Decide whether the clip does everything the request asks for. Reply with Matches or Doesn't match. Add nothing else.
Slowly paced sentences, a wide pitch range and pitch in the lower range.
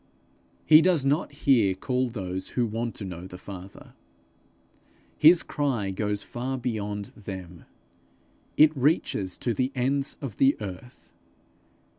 Matches